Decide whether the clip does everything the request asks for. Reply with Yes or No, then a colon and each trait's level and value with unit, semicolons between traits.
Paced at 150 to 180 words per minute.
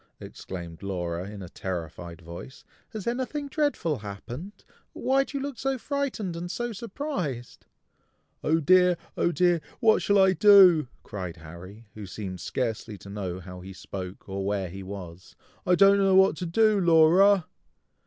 Yes: average, 160 wpm